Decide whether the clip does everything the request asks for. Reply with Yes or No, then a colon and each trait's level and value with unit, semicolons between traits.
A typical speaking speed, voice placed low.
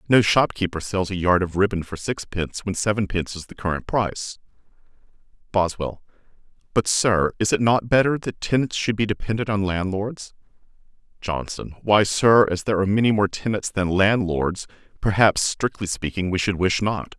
Yes: average, 170 wpm; low, 100 Hz